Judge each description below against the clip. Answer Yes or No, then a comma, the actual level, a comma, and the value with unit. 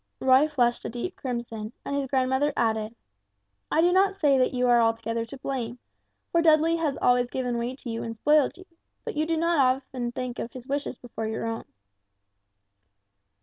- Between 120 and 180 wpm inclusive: No, average, 190 wpm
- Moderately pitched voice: No, very high, 255 Hz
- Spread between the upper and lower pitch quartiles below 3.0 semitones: No, average, 3.8 semitones